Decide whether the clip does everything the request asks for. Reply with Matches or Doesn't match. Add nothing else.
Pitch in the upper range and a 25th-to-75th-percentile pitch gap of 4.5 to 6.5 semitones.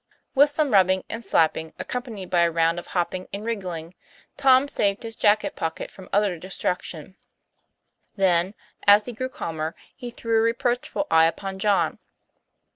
Matches